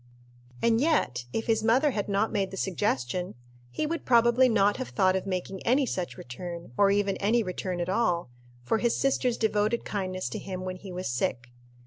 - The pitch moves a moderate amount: Yes, average, 3.9 semitones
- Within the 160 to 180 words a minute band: No, average, 190 wpm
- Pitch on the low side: No, high, 200 Hz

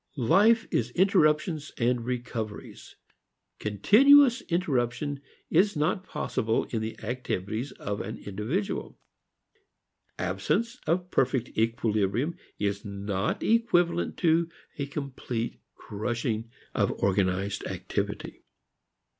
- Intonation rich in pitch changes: Yes, wide, 7.8 semitones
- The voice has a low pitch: Yes, low, 125 Hz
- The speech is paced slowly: Yes, slow, 95 wpm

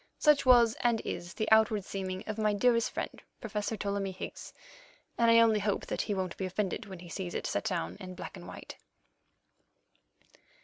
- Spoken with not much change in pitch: No, average, 3.0 semitones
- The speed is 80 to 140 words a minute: No, average, 185 wpm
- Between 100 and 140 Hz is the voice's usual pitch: No, high, 205 Hz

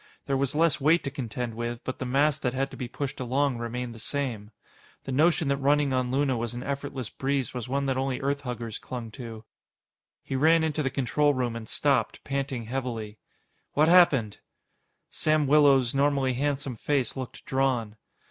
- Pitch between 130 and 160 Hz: Yes, low, 135 Hz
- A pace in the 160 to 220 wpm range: Yes, average, 180 wpm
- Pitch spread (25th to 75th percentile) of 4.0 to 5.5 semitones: No, narrow, 2.6 semitones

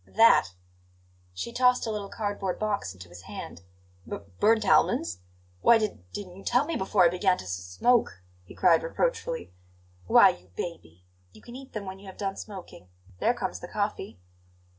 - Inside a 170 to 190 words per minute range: Yes, average, 180 wpm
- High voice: Yes, high, 195 Hz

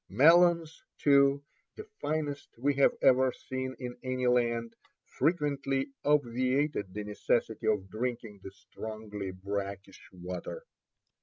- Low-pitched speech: Yes, low, 125 Hz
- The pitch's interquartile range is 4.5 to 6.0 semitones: Yes, average, 5.3 semitones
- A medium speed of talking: No, slow, 110 wpm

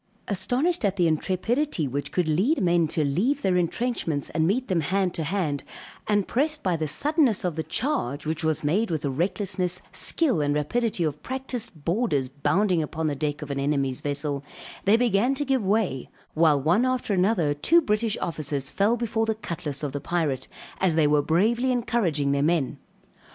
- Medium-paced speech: Yes, average, 185 wpm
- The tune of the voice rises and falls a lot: Yes, wide, 7.1 semitones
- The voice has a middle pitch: Yes, medium, 175 Hz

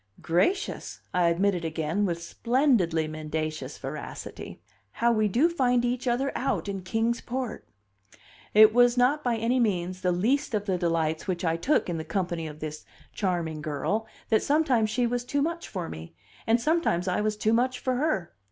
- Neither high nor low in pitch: No, high, 210 Hz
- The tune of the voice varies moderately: No, wide, 6.4 semitones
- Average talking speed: Yes, average, 180 wpm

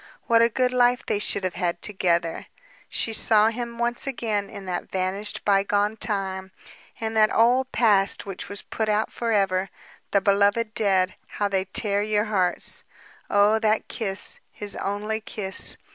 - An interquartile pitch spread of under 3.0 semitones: Yes, narrow, 2.4 semitones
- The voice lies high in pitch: Yes, high, 205 Hz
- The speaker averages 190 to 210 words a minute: No, average, 160 wpm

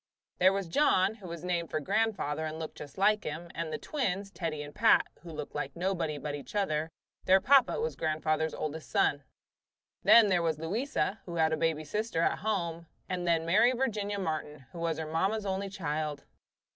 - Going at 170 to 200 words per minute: Yes, average, 195 wpm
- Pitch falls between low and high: Yes, medium, 170 Hz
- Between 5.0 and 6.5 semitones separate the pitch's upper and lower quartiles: No, average, 4.2 semitones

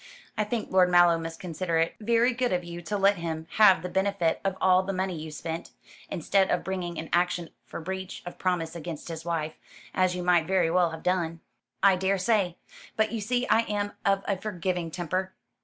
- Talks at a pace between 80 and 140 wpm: No, fast, 205 wpm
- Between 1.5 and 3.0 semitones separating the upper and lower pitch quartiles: Yes, narrow, 2.6 semitones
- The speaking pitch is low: No, medium, 180 Hz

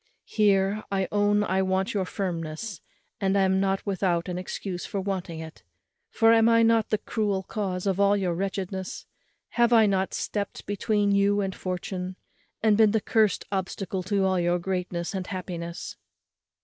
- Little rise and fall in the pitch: Yes, narrow, 2.0 semitones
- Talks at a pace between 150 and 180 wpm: Yes, average, 165 wpm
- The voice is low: No, high, 195 Hz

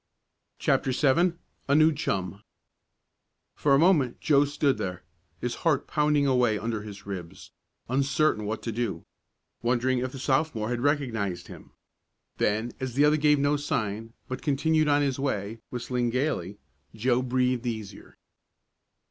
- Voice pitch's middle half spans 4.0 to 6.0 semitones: Yes, average, 4.5 semitones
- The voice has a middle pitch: No, low, 130 Hz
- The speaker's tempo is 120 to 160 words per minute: Yes, average, 145 wpm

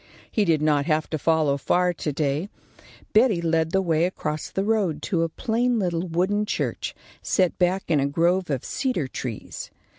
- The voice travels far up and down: No, average, 3.8 semitones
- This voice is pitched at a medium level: Yes, medium, 170 Hz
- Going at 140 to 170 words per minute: No, average, 180 wpm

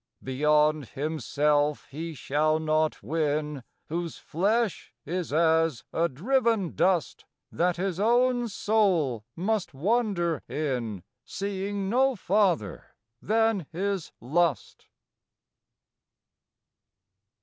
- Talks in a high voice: No, medium, 165 Hz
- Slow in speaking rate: Yes, slow, 90 wpm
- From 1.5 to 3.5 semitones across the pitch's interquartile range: No, average, 5.1 semitones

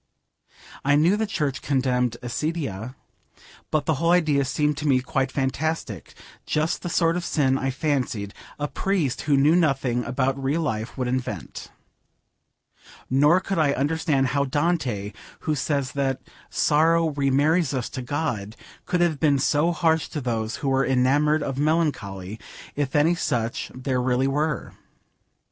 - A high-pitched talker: No, medium, 140 Hz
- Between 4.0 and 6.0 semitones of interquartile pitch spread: No, average, 3.4 semitones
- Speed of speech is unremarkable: Yes, average, 150 wpm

